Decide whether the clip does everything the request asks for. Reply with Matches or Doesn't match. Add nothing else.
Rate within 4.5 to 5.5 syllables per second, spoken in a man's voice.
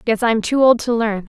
Doesn't match